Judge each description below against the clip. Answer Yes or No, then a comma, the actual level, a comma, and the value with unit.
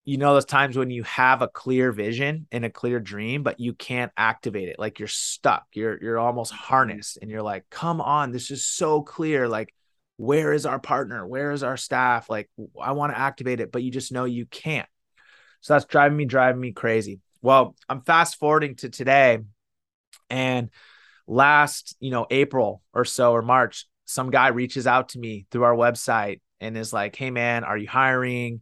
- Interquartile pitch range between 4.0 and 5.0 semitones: No, average, 3.2 semitones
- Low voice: Yes, low, 125 Hz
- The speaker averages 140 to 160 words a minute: No, average, 200 wpm